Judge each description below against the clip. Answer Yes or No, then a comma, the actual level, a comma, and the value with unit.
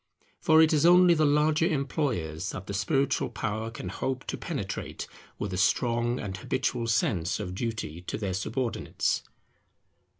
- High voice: No, low, 115 Hz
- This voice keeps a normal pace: Yes, average, 155 wpm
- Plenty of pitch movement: Yes, wide, 7.1 semitones